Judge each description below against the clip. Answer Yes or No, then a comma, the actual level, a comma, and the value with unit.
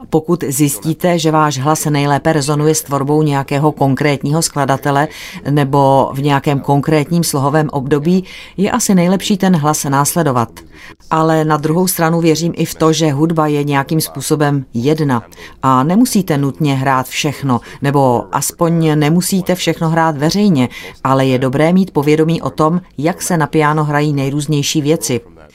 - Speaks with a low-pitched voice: No, medium, 150 Hz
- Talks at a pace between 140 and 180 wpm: Yes, average, 150 wpm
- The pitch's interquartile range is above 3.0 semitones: No, average, 2.7 semitones